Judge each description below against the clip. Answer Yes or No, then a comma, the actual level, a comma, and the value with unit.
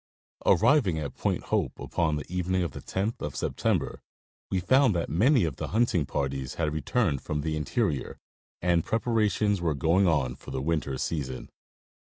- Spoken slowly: No, average, 170 wpm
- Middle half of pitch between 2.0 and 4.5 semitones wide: No, average, 5.3 semitones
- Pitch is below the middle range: Yes, very low, 85 Hz